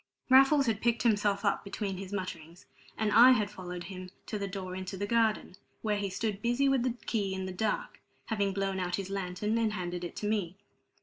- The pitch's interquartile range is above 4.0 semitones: No, average, 2.9 semitones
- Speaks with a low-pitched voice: No, high, 200 Hz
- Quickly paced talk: Yes, fast, 210 wpm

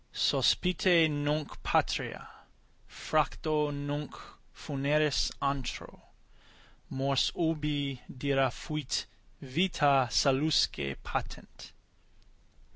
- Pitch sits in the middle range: Yes, medium, 145 Hz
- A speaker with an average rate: No, slow, 65 wpm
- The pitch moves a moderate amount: No, narrow, 1.9 semitones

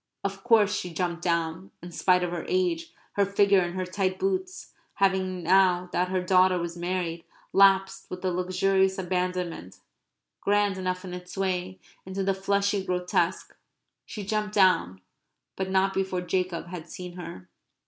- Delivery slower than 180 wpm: Yes, average, 160 wpm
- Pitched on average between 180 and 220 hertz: Yes, medium, 185 Hz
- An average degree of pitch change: No, narrow, 1.5 semitones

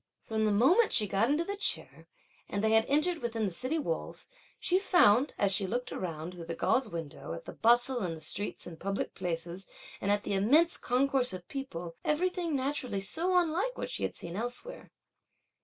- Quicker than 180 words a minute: Yes, average, 195 wpm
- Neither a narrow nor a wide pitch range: No, wide, 7.9 semitones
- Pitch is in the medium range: No, high, 230 Hz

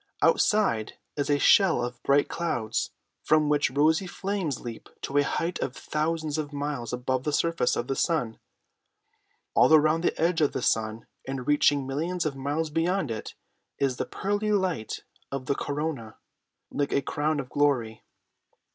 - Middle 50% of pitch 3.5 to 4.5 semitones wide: Yes, average, 3.8 semitones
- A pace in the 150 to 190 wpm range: Yes, average, 165 wpm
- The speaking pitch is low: No, medium, 145 Hz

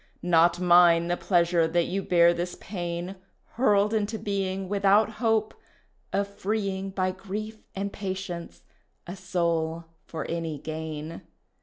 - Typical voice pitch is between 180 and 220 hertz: Yes, medium, 185 Hz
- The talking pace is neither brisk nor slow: No, slow, 130 wpm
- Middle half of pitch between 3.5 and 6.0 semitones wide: No, average, 2.8 semitones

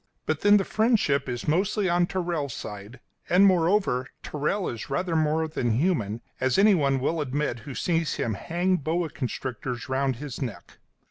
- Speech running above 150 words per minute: Yes, average, 160 wpm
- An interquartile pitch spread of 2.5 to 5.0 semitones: No, wide, 5.5 semitones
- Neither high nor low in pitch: Yes, medium, 150 Hz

